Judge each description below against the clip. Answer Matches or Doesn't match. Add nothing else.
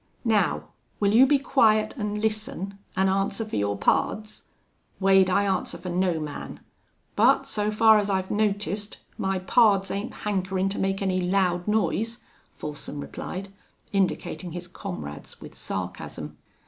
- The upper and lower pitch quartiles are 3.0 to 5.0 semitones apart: Doesn't match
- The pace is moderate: Matches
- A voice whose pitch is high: Matches